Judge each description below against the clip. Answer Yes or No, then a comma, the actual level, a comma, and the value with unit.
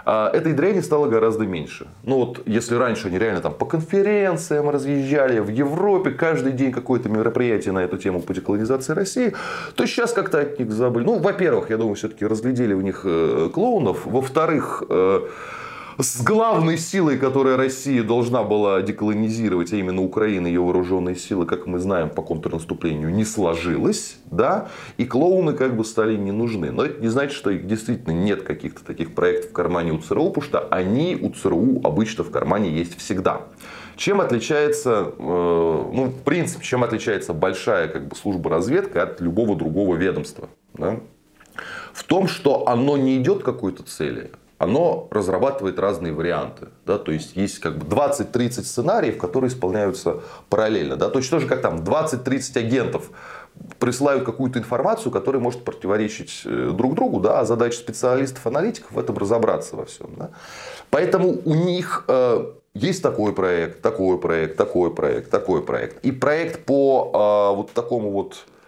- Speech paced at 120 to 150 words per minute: No, fast, 160 wpm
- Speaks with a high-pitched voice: No, low, 120 Hz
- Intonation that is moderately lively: No, wide, 6.6 semitones